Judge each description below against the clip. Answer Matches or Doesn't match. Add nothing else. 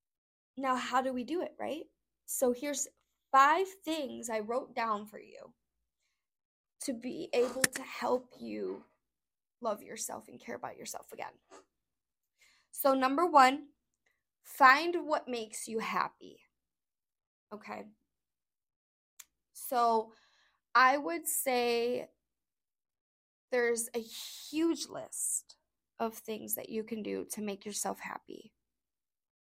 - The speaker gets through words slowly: Matches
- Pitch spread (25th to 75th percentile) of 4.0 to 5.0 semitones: Matches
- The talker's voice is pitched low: Doesn't match